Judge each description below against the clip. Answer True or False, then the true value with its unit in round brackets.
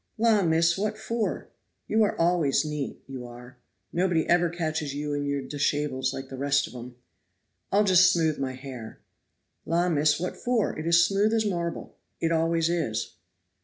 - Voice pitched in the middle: True (160 Hz)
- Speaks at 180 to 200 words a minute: False (170 wpm)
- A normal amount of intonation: True (4.2 semitones)